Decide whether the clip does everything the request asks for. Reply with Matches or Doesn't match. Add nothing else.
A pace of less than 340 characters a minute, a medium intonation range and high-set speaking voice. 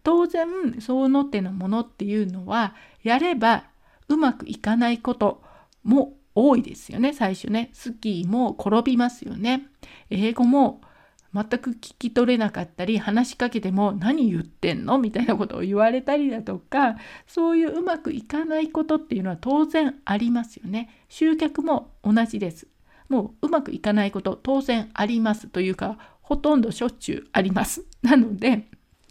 Matches